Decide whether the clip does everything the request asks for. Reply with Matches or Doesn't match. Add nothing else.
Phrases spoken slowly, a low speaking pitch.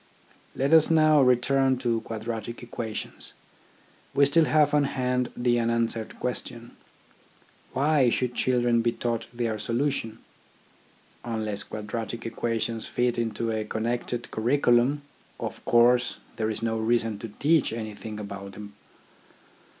Matches